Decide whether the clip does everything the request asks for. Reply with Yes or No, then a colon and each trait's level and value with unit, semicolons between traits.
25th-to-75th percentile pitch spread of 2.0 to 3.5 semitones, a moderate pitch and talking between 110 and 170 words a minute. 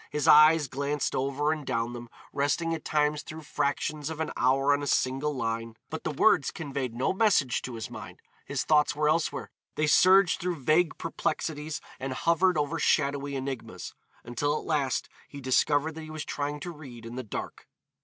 No: average, 2.8 semitones; medium, 145 Hz; average, 185 wpm